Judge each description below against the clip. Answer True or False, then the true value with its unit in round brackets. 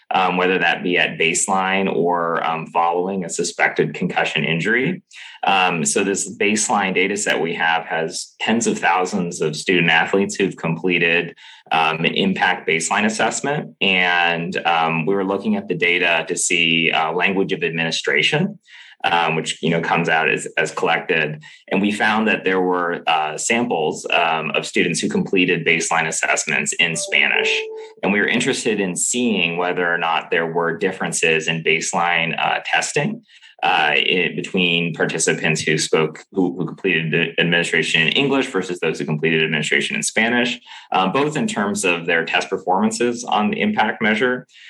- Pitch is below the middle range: True (90 Hz)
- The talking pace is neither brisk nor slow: True (165 wpm)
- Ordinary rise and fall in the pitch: True (4.1 semitones)